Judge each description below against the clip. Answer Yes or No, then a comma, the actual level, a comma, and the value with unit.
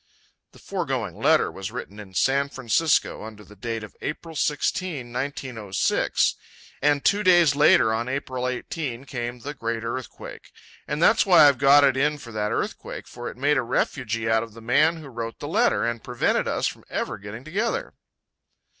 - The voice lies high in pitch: No, low, 130 Hz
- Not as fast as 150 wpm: No, average, 180 wpm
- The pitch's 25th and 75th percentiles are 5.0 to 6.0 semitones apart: No, average, 4.4 semitones